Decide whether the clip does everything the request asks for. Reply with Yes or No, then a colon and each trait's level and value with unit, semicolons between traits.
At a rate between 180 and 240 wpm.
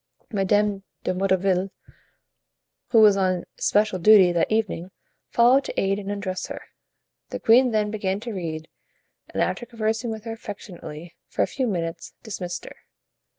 No: average, 150 wpm